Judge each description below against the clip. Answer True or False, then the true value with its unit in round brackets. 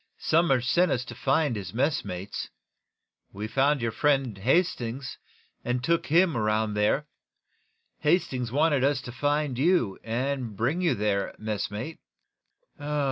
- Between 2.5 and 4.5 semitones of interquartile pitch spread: False (5.2 semitones)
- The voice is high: False (130 Hz)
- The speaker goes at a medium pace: False (130 wpm)